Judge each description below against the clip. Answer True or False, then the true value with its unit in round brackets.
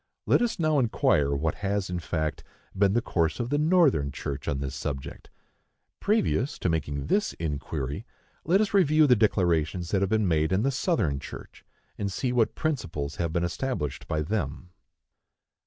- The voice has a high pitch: False (95 Hz)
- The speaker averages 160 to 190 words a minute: True (170 wpm)